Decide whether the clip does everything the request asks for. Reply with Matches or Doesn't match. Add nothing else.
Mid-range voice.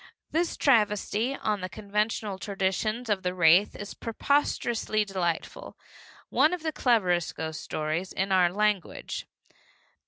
Doesn't match